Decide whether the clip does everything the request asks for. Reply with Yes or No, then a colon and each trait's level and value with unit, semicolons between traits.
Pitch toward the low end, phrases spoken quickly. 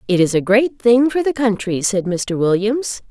No: high, 220 Hz; fast, 210 wpm